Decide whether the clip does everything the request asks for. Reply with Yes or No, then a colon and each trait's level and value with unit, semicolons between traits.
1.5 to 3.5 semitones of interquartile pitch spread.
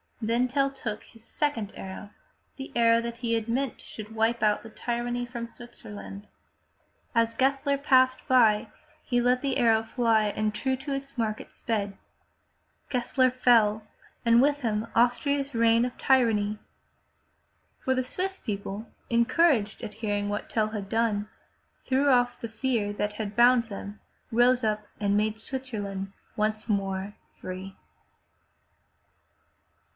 Yes: average, 3.1 semitones